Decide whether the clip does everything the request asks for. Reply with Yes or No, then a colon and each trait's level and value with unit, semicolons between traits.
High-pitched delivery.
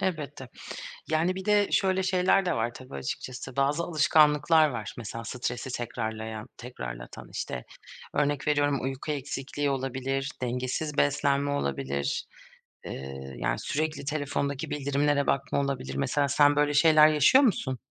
No: medium, 140 Hz